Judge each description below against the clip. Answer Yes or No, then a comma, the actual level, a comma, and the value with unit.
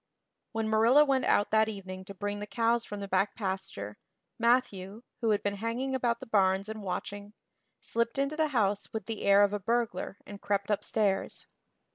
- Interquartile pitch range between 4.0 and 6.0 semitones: No, average, 2.8 semitones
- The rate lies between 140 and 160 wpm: No, average, 185 wpm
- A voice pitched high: Yes, high, 210 Hz